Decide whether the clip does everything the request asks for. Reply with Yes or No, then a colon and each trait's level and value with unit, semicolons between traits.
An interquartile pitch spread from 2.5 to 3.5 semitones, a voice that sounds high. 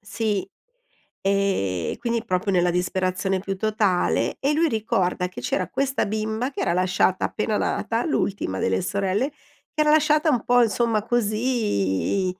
No: average, 4.4 semitones; high, 205 Hz